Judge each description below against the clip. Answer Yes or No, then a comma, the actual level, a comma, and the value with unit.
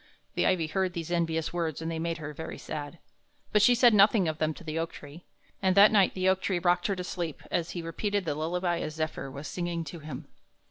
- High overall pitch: No, medium, 170 Hz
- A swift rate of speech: Yes, fast, 240 wpm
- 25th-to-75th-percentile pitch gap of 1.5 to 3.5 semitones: Yes, average, 2.8 semitones